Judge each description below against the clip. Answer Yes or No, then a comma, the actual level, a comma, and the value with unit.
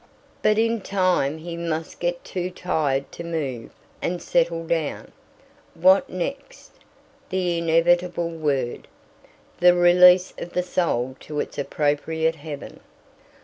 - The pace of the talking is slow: Yes, slow, 120 wpm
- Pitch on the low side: No, medium, 170 Hz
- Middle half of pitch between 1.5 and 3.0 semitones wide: Yes, narrow, 2.4 semitones